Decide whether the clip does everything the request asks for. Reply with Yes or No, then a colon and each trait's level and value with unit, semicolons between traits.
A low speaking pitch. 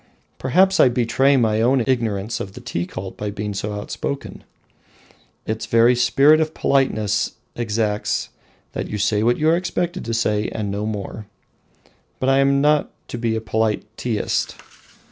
Yes: low, 115 Hz